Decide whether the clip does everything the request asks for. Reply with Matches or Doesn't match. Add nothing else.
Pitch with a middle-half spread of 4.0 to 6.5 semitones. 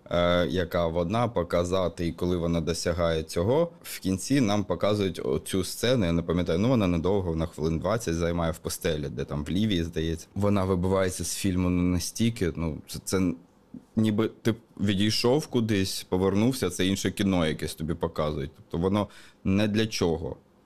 Doesn't match